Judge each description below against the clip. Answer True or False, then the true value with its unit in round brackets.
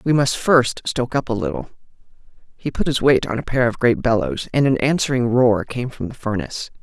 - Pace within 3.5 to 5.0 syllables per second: False (5.6 syllables/s)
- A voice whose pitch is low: True (115 Hz)